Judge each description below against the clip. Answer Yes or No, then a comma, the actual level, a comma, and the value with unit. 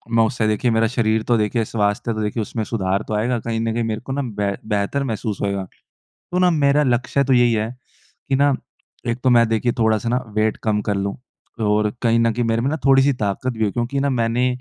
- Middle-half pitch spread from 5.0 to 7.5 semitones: No, average, 2.7 semitones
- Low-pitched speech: Yes, low, 115 Hz